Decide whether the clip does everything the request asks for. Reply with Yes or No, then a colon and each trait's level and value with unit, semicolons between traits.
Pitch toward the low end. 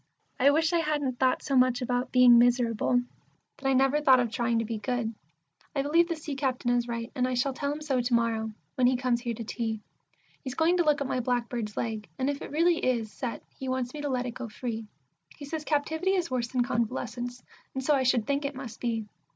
No: very high, 255 Hz